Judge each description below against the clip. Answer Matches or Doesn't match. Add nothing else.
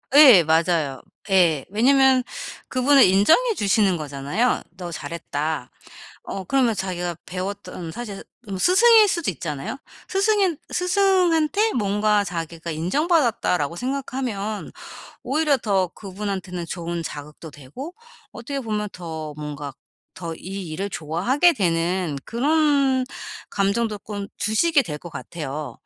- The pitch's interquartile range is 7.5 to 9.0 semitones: Matches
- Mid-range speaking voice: Doesn't match